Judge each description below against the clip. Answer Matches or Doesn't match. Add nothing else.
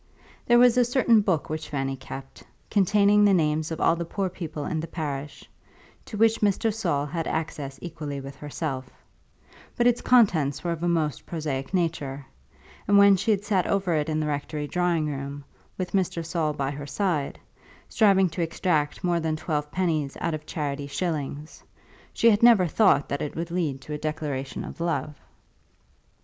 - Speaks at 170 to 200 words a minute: Matches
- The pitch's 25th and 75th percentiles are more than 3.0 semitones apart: Matches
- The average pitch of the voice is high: Doesn't match